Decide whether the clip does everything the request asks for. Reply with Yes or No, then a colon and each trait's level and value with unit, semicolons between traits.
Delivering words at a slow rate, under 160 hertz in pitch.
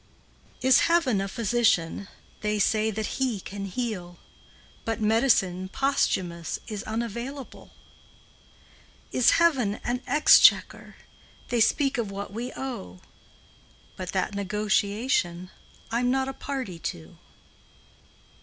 No: slow, 115 wpm; high, 220 Hz